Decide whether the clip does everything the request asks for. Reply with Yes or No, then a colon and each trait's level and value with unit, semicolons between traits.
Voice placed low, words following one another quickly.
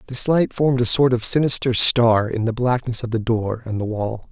Yes: low, 120 Hz; fast, 235 wpm